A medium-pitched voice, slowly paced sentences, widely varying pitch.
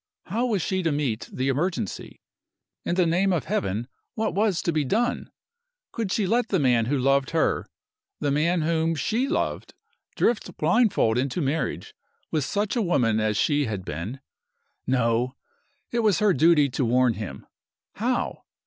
No: medium, 150 Hz; average, 165 wpm; wide, 7.1 semitones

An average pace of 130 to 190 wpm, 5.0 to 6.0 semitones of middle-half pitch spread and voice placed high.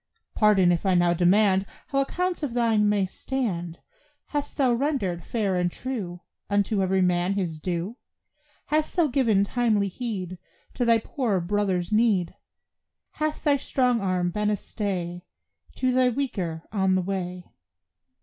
Yes: average, 150 wpm; average, 5.3 semitones; high, 200 Hz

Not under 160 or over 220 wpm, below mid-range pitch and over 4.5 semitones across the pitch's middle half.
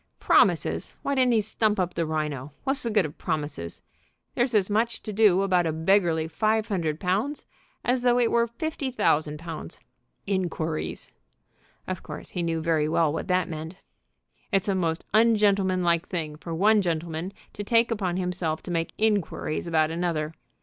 No: average, 170 wpm; medium, 180 Hz; average, 4.9 semitones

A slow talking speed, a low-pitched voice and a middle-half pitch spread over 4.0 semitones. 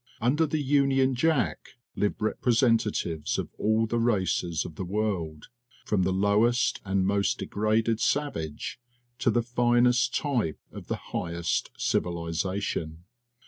Yes: slow, 130 wpm; low, 110 Hz; average, 5.1 semitones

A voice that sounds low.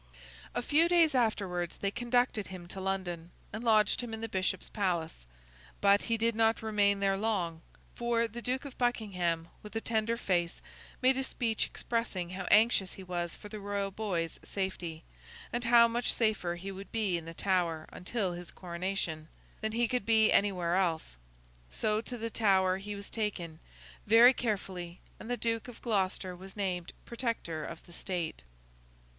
No: high, 200 Hz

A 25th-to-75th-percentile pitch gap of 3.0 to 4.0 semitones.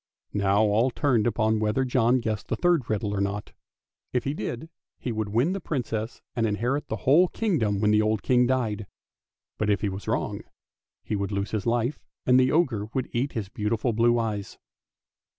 Yes: average, 3.4 semitones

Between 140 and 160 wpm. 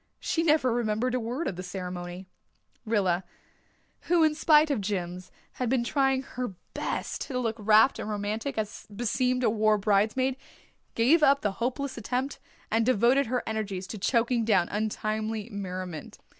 Yes: average, 155 wpm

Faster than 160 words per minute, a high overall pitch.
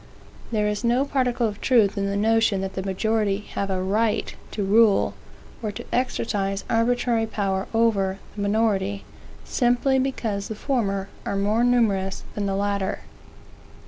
No: average, 150 wpm; high, 210 Hz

